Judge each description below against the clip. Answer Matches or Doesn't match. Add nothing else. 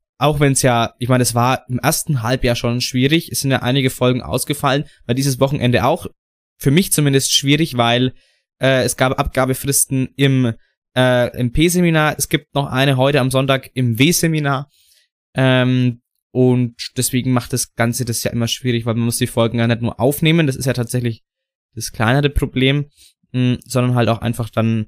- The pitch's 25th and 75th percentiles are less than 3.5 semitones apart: Matches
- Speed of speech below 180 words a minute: Doesn't match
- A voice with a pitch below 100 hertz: Doesn't match